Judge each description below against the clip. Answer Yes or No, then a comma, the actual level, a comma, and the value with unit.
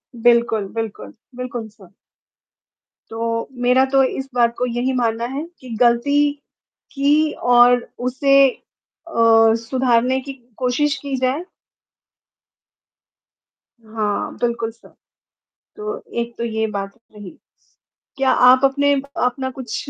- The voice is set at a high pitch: Yes, high, 245 Hz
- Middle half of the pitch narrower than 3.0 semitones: Yes, narrow, 2.6 semitones